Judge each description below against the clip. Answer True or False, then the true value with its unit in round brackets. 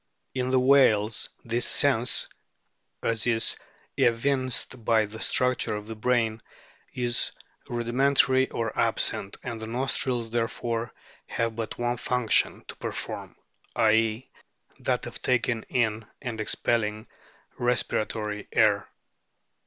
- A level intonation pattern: True (2.1 semitones)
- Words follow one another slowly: True (115 wpm)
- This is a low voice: True (115 Hz)